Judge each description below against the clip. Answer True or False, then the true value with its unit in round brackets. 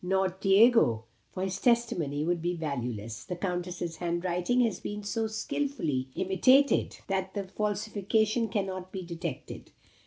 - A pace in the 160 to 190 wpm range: False (135 wpm)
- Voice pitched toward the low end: False (190 Hz)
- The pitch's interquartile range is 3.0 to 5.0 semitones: True (3.8 semitones)